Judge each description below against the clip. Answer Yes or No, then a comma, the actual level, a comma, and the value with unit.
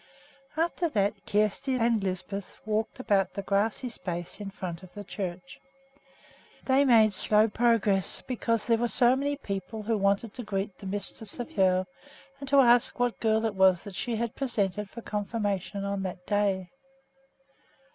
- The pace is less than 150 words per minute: No, average, 165 wpm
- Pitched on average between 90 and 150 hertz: No, high, 210 Hz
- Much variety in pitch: No, average, 3.2 semitones